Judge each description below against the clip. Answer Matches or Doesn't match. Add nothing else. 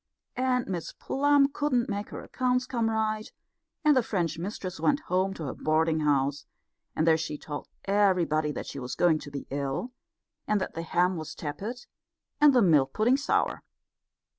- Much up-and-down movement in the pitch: Matches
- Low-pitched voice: Doesn't match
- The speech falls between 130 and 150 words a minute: Doesn't match